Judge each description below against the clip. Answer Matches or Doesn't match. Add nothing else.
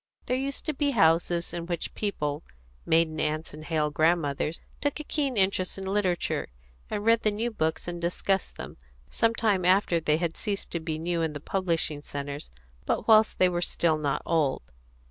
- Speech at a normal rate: Matches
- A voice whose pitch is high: Doesn't match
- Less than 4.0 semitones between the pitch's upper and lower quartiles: Doesn't match